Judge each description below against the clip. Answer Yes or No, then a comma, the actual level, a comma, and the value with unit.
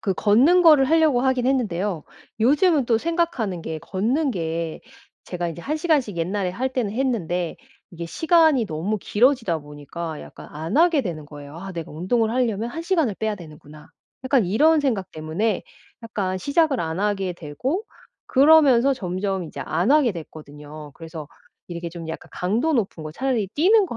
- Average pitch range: No, wide, 8.1 semitones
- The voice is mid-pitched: No, high, 210 Hz